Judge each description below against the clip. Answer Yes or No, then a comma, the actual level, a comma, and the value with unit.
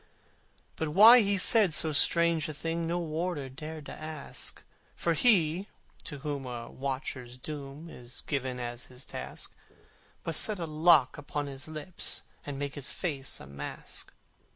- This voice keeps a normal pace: Yes, average, 155 wpm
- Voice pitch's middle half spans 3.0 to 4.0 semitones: Yes, average, 3.7 semitones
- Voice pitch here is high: No, medium, 150 Hz